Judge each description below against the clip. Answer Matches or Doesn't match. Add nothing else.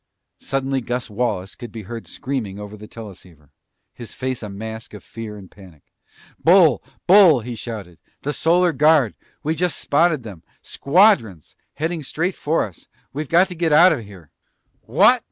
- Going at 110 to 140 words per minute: Doesn't match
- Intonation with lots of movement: Matches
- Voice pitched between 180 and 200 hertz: Doesn't match